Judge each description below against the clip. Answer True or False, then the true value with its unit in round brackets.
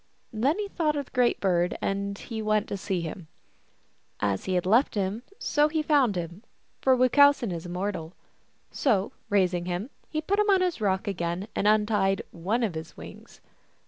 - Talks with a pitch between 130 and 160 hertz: False (205 Hz)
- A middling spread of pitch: False (6.0 semitones)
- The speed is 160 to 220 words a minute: True (175 wpm)